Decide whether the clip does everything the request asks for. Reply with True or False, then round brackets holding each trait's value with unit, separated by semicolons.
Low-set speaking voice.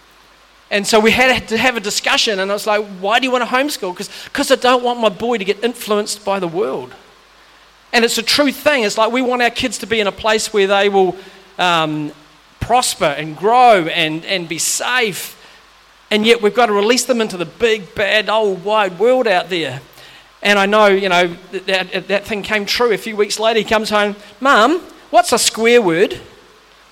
False (215 Hz)